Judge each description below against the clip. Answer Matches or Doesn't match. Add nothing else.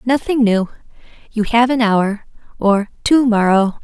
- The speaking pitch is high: Matches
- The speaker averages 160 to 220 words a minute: Doesn't match